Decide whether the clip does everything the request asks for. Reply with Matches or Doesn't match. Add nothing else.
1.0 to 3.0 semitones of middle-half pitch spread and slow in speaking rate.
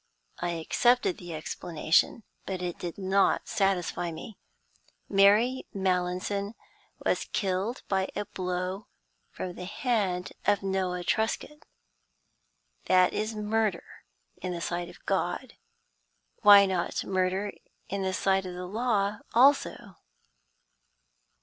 Matches